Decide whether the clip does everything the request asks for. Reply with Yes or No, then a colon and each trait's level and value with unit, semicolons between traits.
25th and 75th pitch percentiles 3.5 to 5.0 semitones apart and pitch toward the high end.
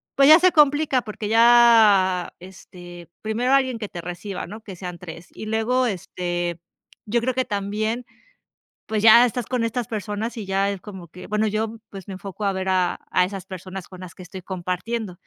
Yes: average, 3.9 semitones; high, 205 Hz